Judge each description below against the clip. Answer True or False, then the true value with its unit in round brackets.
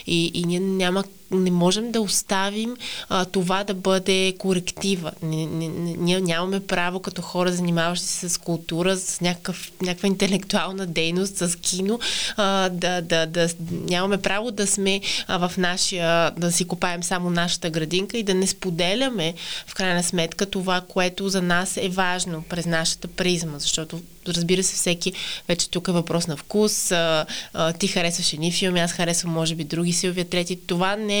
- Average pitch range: False (1.9 semitones)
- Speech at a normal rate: False (170 wpm)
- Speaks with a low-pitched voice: False (180 Hz)